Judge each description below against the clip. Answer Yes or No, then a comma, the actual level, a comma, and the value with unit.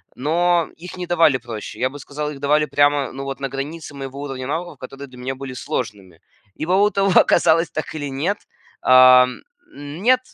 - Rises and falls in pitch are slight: No, average, 4.1 semitones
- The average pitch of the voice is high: No, medium, 140 Hz